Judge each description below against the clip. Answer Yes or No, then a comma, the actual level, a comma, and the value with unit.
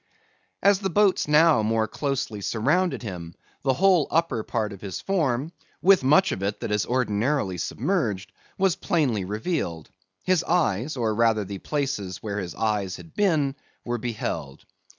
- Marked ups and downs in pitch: Yes, wide, 7.9 semitones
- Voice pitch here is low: Yes, low, 120 Hz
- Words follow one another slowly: No, average, 155 wpm